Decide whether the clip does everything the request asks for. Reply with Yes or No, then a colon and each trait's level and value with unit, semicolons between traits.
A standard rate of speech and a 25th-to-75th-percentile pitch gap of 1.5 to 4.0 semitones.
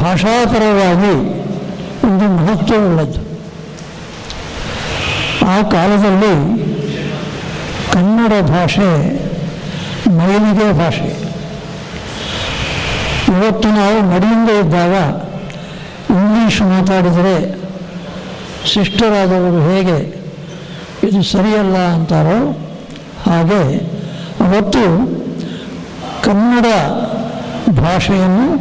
No: slow, 50 wpm; average, 3.0 semitones